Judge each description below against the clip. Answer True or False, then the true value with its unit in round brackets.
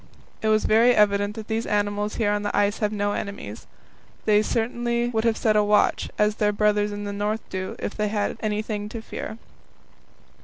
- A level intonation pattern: True (1.1 semitones)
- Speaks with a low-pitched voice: False (210 Hz)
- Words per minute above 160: True (200 wpm)